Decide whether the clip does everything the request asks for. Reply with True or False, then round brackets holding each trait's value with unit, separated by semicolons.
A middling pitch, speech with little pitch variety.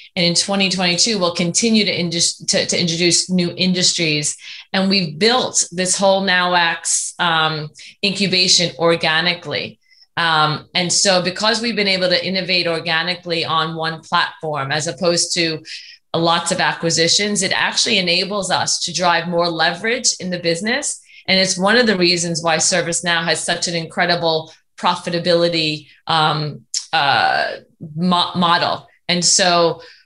True (175 Hz; 2.1 semitones)